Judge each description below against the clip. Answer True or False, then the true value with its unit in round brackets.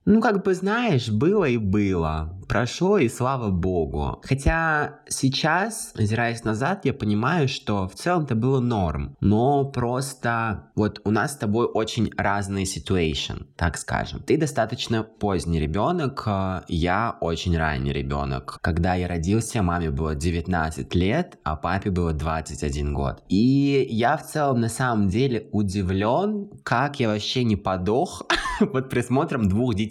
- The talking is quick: False (145 wpm)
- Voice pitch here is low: True (105 Hz)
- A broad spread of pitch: True (7.0 semitones)